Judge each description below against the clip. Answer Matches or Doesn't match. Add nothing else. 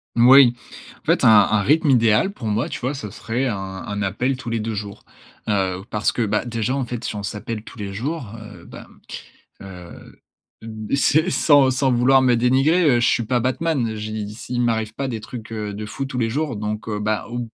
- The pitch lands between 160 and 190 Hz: Doesn't match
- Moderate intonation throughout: Matches